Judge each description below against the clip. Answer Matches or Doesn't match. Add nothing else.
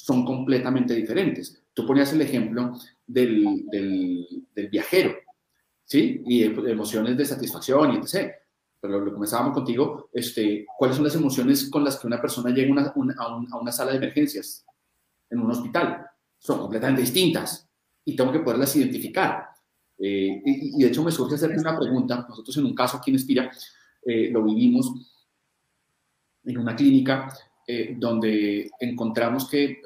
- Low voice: Matches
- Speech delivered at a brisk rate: Doesn't match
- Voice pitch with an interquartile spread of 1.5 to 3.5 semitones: Doesn't match